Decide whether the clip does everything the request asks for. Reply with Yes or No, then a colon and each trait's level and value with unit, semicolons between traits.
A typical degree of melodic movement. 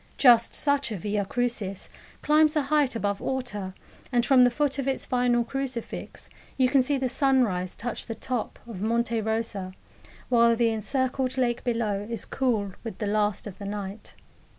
Yes: average, 3.8 semitones